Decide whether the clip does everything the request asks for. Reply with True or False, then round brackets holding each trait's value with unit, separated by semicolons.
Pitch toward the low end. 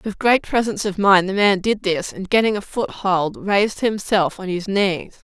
False (195 Hz)